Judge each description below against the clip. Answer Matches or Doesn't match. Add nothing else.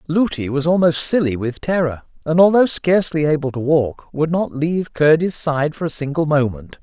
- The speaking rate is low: Doesn't match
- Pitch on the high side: Doesn't match